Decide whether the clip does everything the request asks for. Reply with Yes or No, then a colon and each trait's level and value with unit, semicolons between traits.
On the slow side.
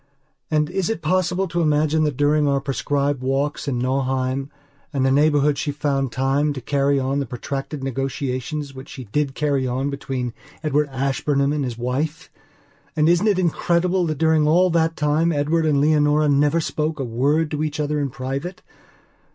No: average, 175 wpm